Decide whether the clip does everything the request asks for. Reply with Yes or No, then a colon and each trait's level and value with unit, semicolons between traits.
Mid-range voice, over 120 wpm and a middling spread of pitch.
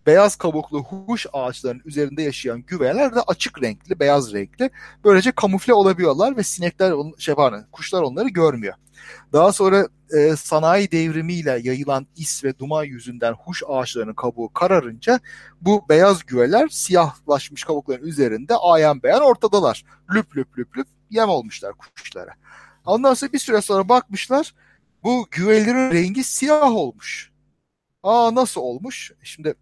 No: medium, 170 Hz; average, 135 wpm; wide, 7.6 semitones